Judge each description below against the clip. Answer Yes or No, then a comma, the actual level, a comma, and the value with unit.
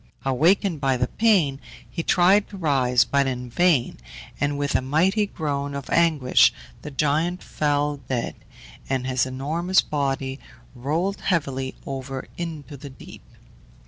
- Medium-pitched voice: Yes, medium, 145 Hz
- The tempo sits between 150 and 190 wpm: No, average, 140 wpm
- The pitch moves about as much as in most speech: Yes, average, 4.2 semitones